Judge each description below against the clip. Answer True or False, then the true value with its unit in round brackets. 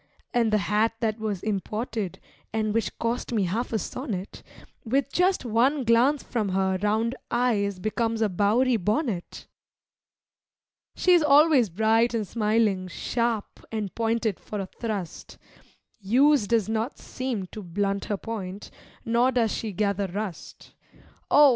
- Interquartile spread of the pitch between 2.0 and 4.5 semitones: True (2.9 semitones)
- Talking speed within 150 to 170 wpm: False (140 wpm)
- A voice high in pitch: True (220 Hz)